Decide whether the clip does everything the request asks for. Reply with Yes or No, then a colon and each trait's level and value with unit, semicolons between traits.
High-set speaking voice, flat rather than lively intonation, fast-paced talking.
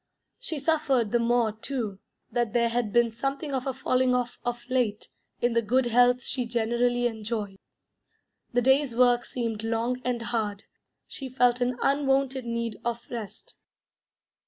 No: high, 240 Hz; narrow, 1.7 semitones; average, 155 wpm